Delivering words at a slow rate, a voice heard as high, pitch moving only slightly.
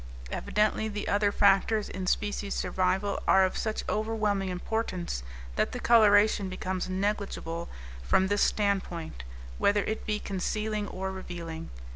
Yes: slow, 130 wpm; high, 200 Hz; narrow, 2.2 semitones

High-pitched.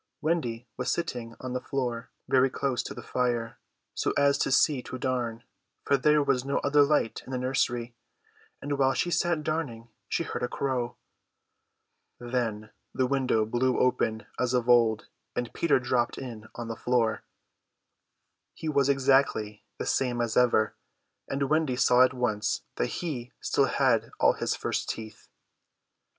No: low, 125 Hz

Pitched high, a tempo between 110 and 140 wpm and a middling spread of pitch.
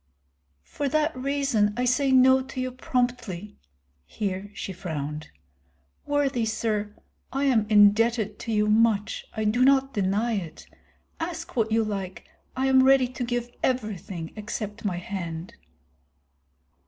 Yes: high, 225 Hz; slow, 135 wpm; average, 4.1 semitones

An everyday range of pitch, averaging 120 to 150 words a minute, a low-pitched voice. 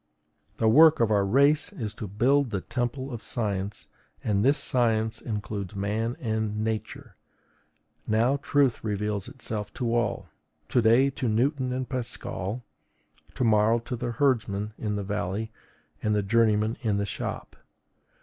Yes: average, 3.0 semitones; average, 145 wpm; low, 110 Hz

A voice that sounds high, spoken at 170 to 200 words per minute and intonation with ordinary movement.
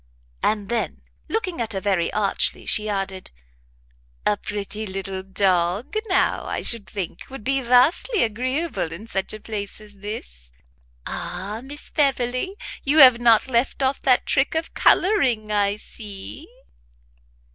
No: high, 215 Hz; average, 140 wpm; average, 5.0 semitones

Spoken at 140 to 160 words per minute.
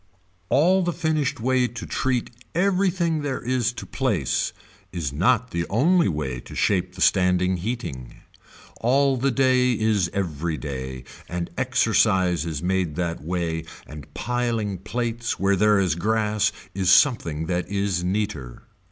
Yes: average, 145 wpm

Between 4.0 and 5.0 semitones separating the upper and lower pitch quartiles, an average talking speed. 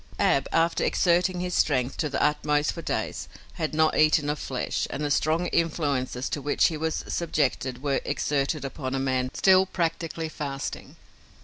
No: average, 3.2 semitones; average, 170 wpm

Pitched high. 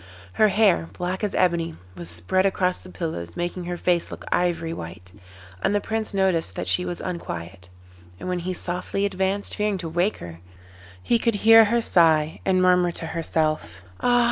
No: medium, 180 Hz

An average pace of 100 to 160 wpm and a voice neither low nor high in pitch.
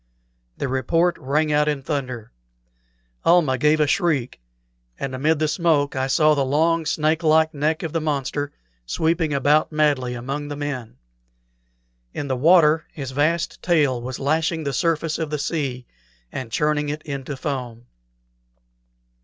Yes: average, 150 wpm; medium, 150 Hz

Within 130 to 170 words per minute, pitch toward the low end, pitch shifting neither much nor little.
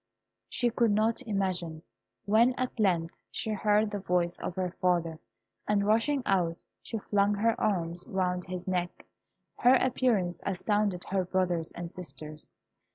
No: average, 145 wpm; high, 190 Hz; average, 3.4 semitones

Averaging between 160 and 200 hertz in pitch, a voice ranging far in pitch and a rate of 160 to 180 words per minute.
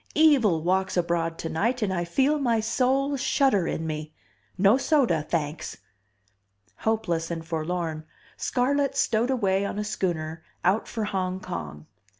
No: high, 190 Hz; wide, 6.6 semitones; average, 140 wpm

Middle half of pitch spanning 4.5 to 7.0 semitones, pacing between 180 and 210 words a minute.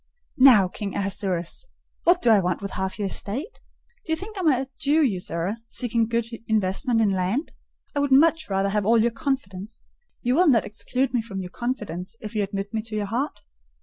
Yes: average, 5.2 semitones; fast, 205 wpm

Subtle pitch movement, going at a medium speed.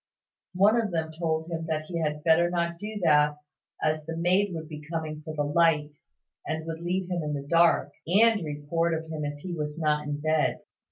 No: narrow, 2.1 semitones; fast, 210 wpm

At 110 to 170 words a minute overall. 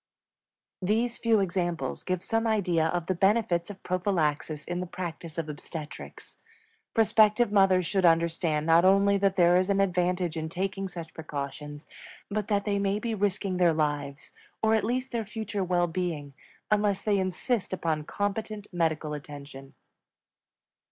Yes: average, 150 wpm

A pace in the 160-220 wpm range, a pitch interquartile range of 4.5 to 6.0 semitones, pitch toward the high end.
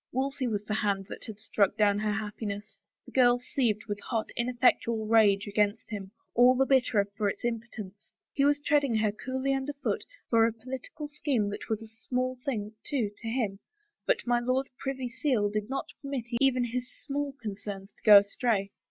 No: average, 190 wpm; average, 3.8 semitones; high, 230 Hz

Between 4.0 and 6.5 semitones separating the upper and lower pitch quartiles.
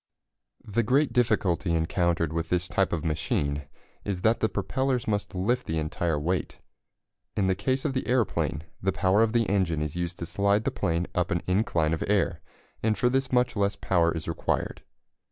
Yes: average, 4.9 semitones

